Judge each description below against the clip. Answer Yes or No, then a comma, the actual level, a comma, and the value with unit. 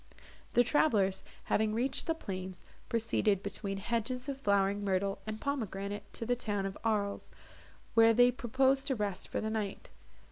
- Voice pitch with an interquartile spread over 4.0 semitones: No, average, 3.5 semitones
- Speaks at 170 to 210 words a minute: No, average, 155 wpm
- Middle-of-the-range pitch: No, high, 215 Hz